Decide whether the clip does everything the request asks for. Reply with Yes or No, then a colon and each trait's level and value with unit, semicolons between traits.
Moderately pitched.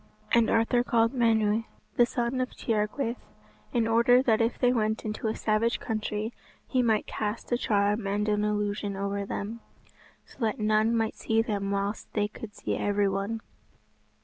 No: high, 220 Hz